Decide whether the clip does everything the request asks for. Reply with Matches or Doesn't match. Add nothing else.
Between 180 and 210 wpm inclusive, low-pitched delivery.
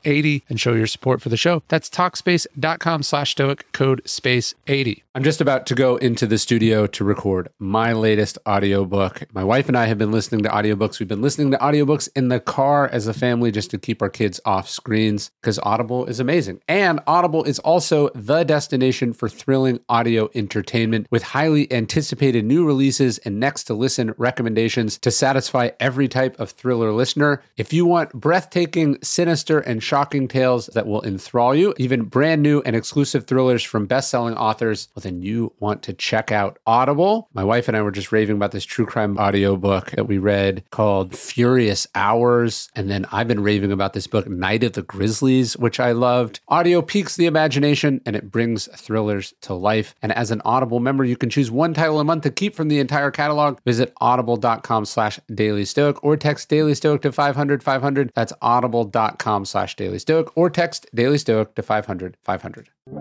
Matches